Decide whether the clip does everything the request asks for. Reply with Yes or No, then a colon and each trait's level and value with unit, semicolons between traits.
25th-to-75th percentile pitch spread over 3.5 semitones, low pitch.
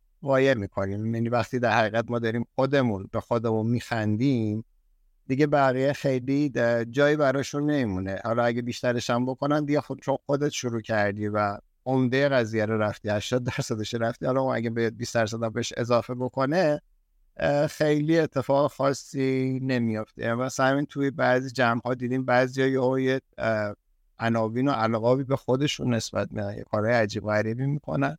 No: average, 3.2 semitones; low, 125 Hz